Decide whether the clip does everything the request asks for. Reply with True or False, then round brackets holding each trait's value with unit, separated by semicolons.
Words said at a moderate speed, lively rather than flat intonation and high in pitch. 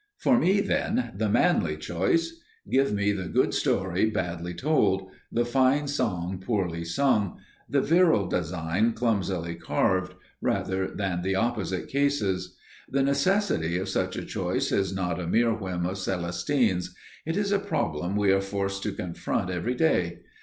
False (155 wpm; 6.6 semitones; 100 Hz)